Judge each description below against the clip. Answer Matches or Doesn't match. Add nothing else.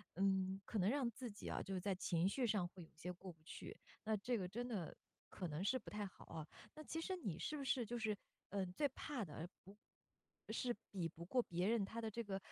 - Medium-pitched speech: Doesn't match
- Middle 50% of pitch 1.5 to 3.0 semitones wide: Doesn't match